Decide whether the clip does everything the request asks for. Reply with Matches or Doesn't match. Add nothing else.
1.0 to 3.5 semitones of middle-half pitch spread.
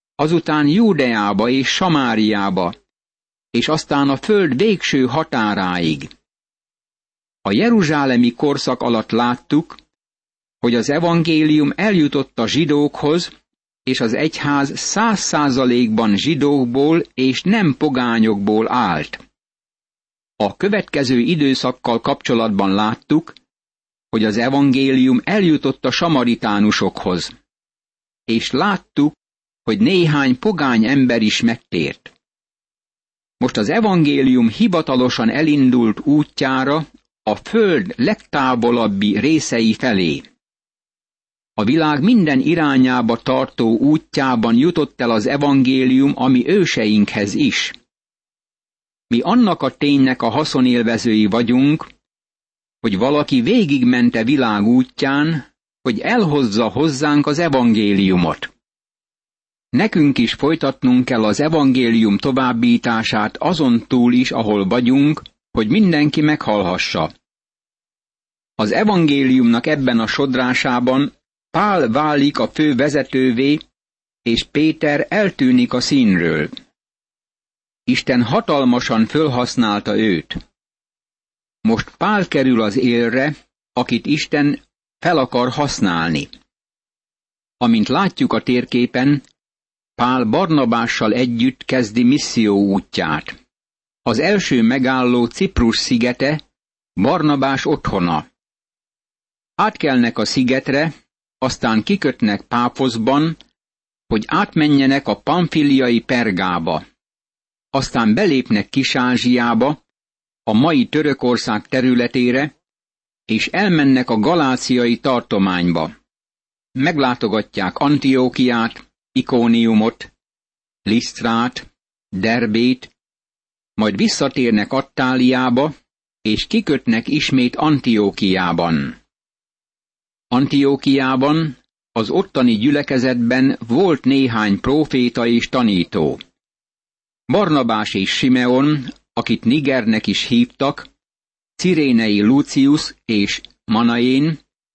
Doesn't match